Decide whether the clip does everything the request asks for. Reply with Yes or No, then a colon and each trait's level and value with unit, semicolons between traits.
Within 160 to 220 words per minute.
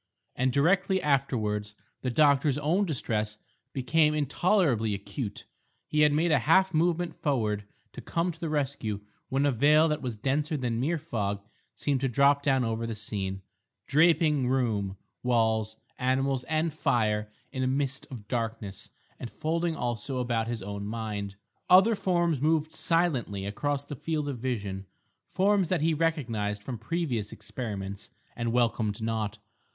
No: average, 150 wpm